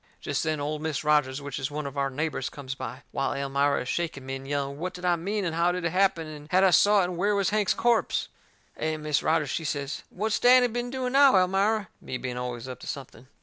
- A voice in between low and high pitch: Yes, medium, 155 Hz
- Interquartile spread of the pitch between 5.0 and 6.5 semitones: Yes, wide, 5.6 semitones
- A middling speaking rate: No, fast, 255 wpm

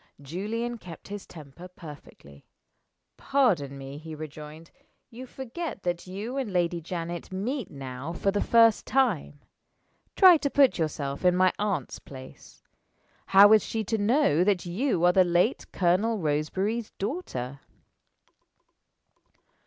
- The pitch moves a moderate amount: No, wide, 6.4 semitones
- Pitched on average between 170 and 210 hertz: Yes, medium, 185 Hz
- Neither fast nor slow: No, slow, 130 wpm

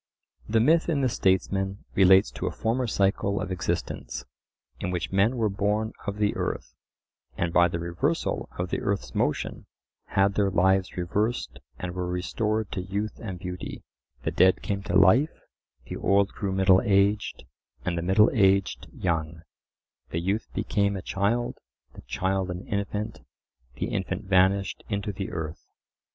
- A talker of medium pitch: No, very low, 95 Hz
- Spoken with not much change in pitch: Yes, narrow, 2.1 semitones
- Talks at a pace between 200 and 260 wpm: No, average, 160 wpm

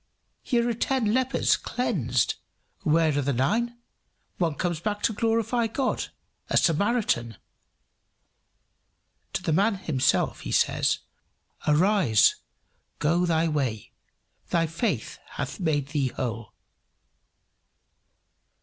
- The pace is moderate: No, slow, 105 wpm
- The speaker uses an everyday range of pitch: No, wide, 7.8 semitones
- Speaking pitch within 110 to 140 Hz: No, medium, 165 Hz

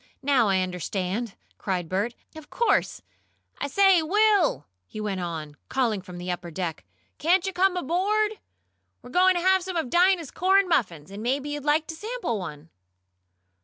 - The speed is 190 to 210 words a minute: No, average, 170 wpm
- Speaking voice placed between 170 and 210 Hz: No, very high, 275 Hz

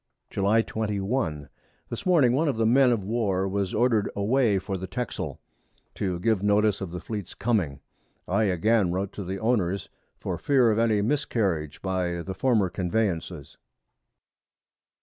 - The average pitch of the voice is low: Yes, low, 100 Hz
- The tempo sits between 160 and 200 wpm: No, average, 150 wpm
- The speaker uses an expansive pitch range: No, average, 3.6 semitones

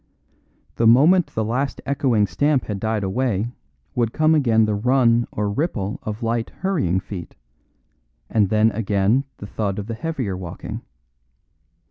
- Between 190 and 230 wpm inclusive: No, average, 145 wpm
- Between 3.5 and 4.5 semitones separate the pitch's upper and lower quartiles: Yes, average, 4.2 semitones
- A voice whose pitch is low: Yes, low, 115 Hz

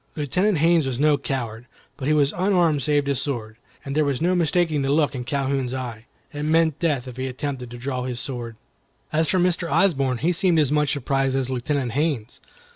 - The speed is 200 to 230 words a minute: Yes, fast, 205 wpm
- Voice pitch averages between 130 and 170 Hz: Yes, medium, 140 Hz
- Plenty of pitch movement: No, average, 3.5 semitones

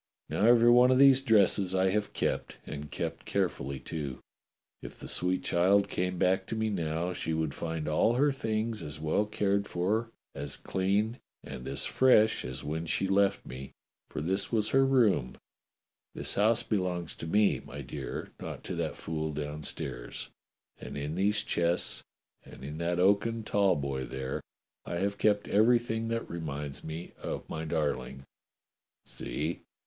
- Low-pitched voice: Yes, very low, 90 Hz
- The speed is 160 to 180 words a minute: Yes, average, 165 wpm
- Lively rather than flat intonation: Yes, wide, 5.8 semitones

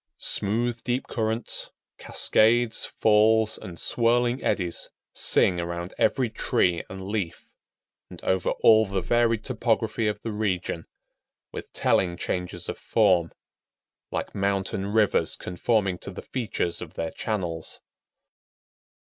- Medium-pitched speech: No, low, 105 Hz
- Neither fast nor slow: No, slow, 120 wpm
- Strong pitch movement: No, average, 4.0 semitones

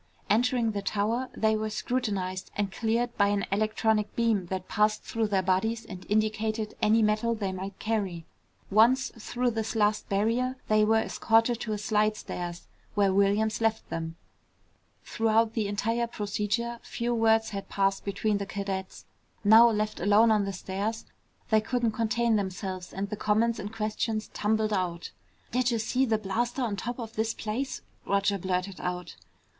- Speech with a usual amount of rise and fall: No, narrow, 2.2 semitones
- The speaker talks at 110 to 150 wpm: No, average, 160 wpm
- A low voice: No, high, 215 Hz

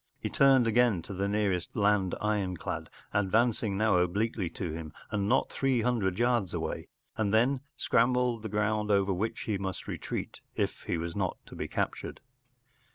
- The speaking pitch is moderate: No, low, 105 Hz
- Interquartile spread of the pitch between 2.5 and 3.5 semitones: Yes, average, 3.2 semitones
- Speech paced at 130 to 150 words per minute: No, average, 165 wpm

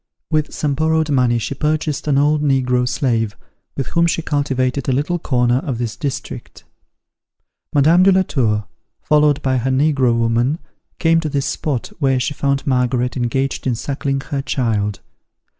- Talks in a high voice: No, low, 135 Hz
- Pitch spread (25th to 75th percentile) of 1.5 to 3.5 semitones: Yes, average, 3.2 semitones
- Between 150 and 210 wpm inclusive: Yes, average, 160 wpm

